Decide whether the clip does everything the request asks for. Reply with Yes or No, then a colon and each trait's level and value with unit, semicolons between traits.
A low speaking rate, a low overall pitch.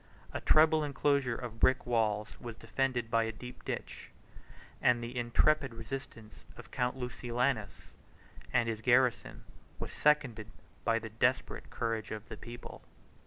No: average, 145 wpm; low, 120 Hz